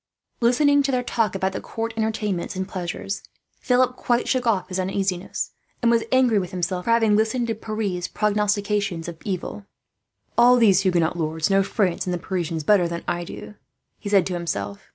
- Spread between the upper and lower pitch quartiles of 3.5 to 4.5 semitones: Yes, average, 4.1 semitones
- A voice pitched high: Yes, high, 200 Hz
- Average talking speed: Yes, average, 185 wpm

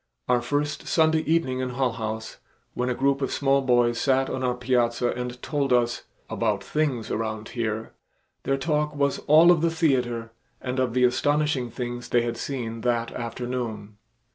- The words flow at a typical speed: Yes, average, 170 wpm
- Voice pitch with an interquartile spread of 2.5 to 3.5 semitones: Yes, average, 2.8 semitones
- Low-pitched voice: Yes, low, 125 Hz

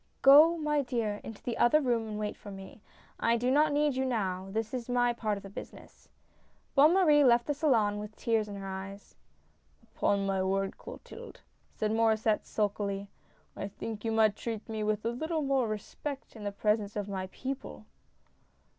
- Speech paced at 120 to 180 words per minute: No, average, 195 wpm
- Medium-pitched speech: No, high, 220 Hz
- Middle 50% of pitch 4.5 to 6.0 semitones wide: No, average, 4.1 semitones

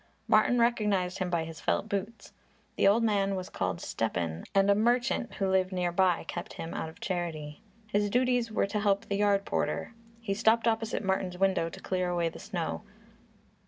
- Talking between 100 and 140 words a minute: No, average, 190 wpm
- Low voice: No, high, 195 Hz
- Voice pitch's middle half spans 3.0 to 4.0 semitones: Yes, average, 3.4 semitones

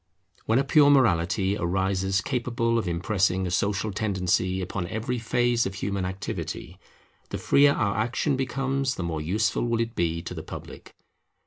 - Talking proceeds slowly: No, average, 160 wpm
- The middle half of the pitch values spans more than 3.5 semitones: Yes, average, 4.5 semitones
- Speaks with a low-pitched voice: Yes, low, 100 Hz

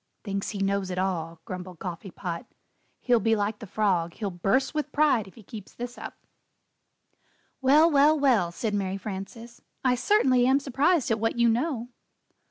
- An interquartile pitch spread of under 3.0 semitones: No, average, 5.1 semitones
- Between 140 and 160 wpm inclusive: No, average, 175 wpm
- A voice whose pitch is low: No, high, 225 Hz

